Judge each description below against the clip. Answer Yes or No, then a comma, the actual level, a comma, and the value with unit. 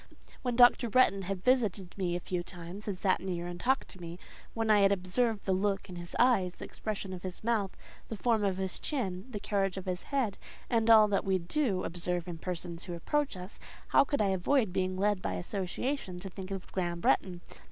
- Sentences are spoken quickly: Yes, fast, 215 wpm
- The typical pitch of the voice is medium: No, high, 195 Hz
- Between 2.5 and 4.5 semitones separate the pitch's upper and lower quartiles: Yes, average, 3.3 semitones